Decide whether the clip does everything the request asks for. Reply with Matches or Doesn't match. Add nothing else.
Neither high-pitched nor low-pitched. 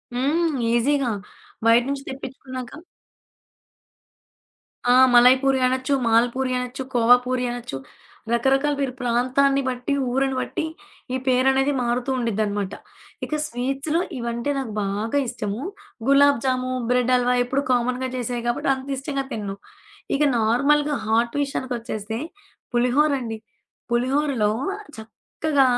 Doesn't match